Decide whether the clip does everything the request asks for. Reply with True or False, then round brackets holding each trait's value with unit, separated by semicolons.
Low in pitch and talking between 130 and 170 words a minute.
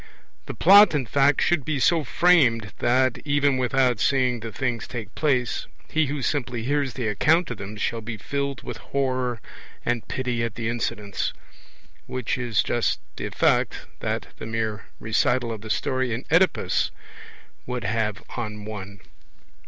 True (125 Hz; 160 wpm)